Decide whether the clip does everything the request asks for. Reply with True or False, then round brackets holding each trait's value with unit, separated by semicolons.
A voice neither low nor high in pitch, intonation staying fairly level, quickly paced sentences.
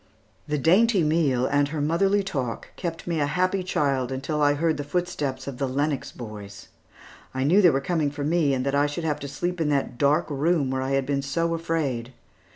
False (145 Hz; 3.4 semitones; 215 wpm)